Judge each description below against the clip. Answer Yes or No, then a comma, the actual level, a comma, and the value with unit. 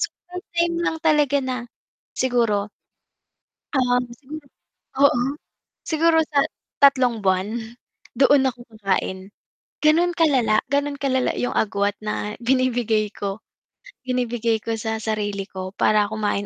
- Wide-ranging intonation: No, average, 5.0 semitones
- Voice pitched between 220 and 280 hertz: Yes, high, 245 Hz